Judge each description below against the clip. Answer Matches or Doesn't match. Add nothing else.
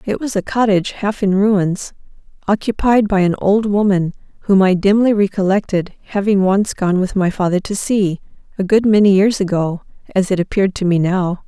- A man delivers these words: Doesn't match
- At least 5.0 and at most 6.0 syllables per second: Matches